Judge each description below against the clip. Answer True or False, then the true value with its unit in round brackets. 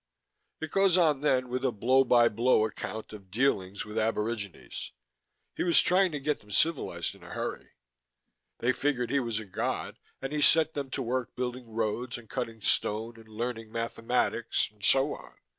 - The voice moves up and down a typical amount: True (3.6 semitones)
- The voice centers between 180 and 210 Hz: False (120 Hz)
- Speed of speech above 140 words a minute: True (180 wpm)